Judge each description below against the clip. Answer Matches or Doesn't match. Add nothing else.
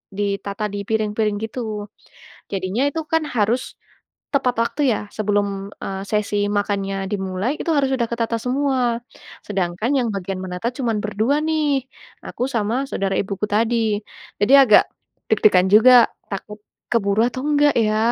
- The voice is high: Matches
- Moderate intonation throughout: Matches